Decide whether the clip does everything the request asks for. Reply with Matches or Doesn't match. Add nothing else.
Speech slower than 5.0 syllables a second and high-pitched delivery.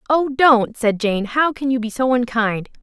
Matches